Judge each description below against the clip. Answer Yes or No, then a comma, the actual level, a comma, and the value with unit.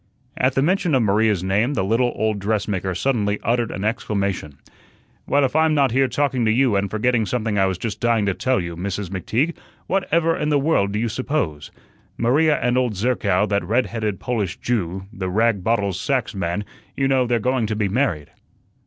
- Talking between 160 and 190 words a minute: No, average, 200 wpm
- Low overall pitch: Yes, low, 110 Hz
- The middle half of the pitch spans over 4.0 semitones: Yes, average, 4.5 semitones